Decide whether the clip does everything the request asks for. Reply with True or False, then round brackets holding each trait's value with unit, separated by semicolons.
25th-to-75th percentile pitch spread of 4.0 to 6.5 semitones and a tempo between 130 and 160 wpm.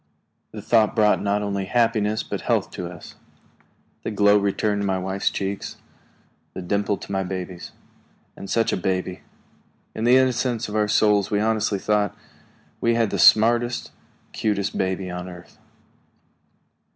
False (2.4 semitones; 150 wpm)